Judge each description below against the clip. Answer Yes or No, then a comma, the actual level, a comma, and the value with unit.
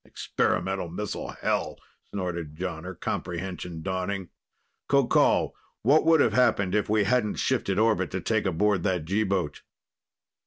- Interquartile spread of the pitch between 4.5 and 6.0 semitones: No, average, 3.3 semitones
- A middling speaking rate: No, slow, 130 wpm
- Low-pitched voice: Yes, very low, 95 Hz